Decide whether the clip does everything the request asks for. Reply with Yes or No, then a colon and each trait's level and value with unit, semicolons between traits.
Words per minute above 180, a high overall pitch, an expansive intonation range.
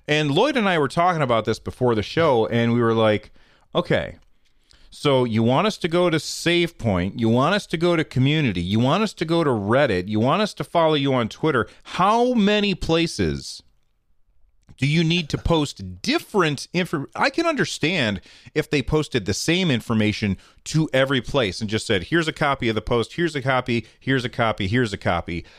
No: average, 200 wpm; low, 135 Hz; wide, 7.0 semitones